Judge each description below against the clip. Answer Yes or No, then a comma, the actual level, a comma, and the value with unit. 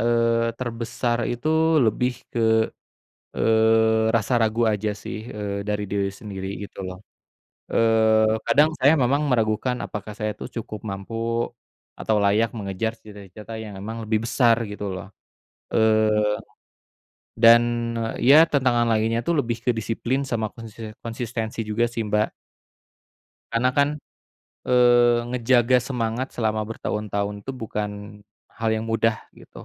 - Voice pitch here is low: Yes, low, 115 Hz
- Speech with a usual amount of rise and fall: No, narrow, 1.8 semitones